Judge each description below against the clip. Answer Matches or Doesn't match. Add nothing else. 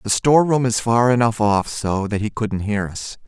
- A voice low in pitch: Matches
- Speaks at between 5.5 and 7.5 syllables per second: Doesn't match